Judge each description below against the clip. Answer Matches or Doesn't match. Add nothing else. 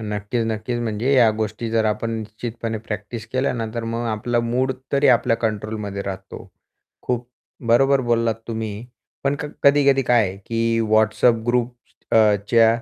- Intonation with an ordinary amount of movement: Doesn't match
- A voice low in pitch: Matches